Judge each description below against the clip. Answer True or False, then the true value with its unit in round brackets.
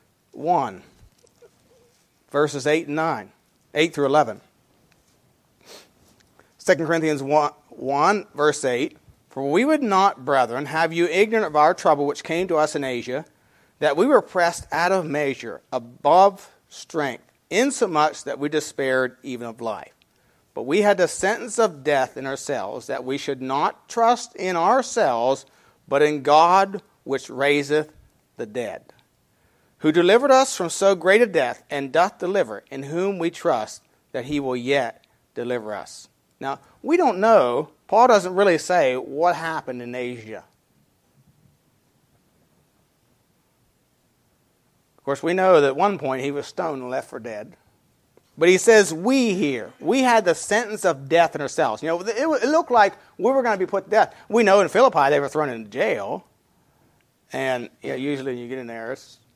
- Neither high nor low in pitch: True (155 Hz)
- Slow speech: False (165 wpm)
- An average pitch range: False (6.2 semitones)